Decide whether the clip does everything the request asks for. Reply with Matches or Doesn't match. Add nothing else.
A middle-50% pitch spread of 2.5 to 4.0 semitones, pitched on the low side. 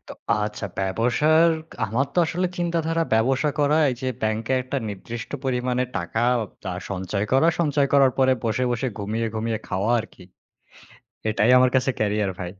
Doesn't match